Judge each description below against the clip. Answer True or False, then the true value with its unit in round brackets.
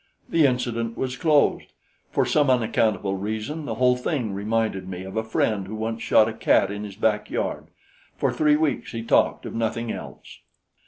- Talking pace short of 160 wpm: False (175 wpm)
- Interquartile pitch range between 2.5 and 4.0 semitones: True (3.1 semitones)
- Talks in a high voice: False (115 Hz)